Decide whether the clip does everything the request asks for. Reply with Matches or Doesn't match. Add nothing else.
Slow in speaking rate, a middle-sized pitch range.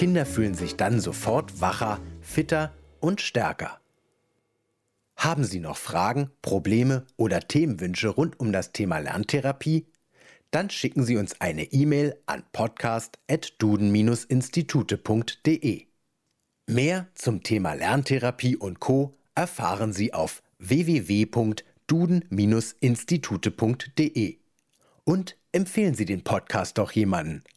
Doesn't match